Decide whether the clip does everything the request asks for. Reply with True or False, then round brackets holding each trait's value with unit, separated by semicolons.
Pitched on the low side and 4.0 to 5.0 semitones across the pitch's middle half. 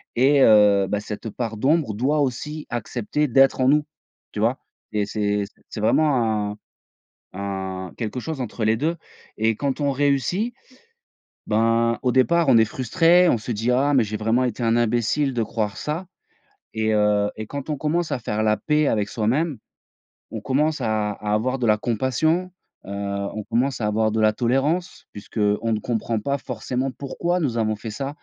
True (120 Hz; 4.6 semitones)